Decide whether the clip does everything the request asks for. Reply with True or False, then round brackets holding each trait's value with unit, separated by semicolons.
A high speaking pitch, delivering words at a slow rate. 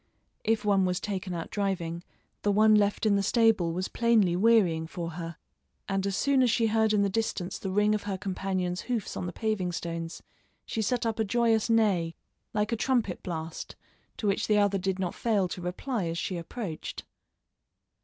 False (200 Hz; 195 wpm)